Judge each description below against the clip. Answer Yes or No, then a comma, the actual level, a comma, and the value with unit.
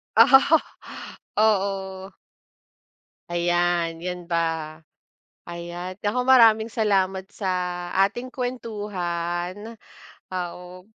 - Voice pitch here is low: No, high, 190 Hz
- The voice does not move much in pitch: No, average, 3.8 semitones